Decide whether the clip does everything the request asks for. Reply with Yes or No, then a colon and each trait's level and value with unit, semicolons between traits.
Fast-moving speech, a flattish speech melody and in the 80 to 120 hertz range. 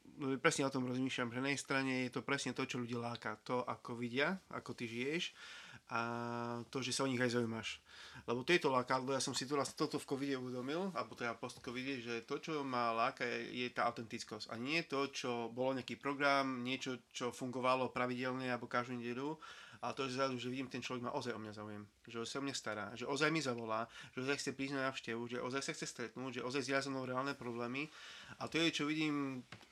No: fast, 220 wpm; narrow, 2.3 semitones; low, 130 Hz